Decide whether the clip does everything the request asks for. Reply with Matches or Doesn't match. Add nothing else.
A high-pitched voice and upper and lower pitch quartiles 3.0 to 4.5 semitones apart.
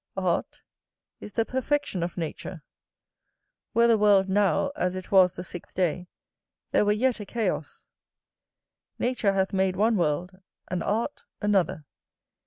Matches